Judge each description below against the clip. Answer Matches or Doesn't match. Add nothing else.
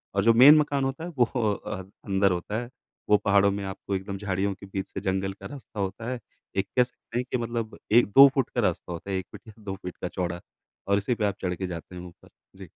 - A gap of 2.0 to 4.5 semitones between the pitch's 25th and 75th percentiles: Matches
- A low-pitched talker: Matches